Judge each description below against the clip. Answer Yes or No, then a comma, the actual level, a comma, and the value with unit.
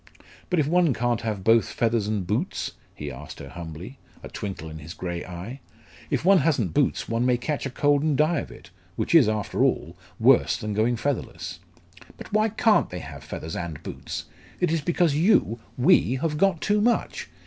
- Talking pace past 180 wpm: Yes, average, 195 wpm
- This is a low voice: Yes, low, 120 Hz